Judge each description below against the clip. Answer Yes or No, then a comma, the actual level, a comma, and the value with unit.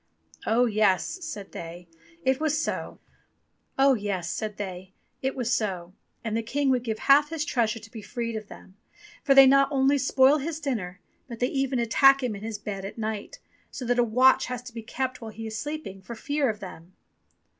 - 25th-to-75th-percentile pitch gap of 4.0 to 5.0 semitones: Yes, average, 4.3 semitones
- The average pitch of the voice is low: No, high, 235 Hz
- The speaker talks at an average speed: Yes, average, 180 wpm